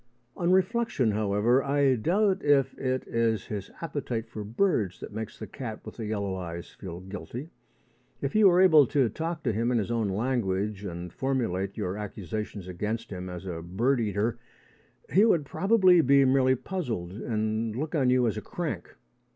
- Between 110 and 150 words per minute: No, average, 175 wpm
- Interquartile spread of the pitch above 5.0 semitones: Yes, wide, 5.5 semitones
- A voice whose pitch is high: No, low, 115 Hz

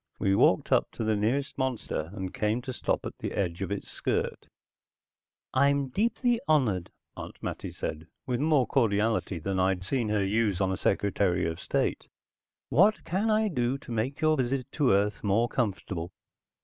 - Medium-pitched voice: No, low, 110 Hz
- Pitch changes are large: Yes, wide, 5.9 semitones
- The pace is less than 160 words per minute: No, average, 175 wpm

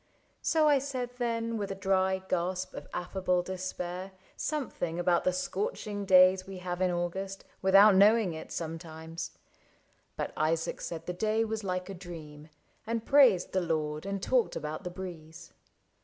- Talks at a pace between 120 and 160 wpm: Yes, average, 155 wpm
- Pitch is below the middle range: No, medium, 185 Hz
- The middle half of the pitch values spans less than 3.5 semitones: Yes, average, 2.9 semitones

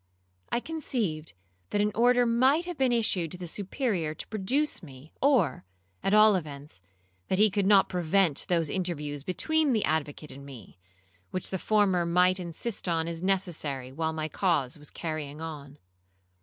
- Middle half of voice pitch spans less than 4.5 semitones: No, wide, 5.5 semitones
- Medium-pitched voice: Yes, medium, 180 Hz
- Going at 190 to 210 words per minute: No, average, 165 wpm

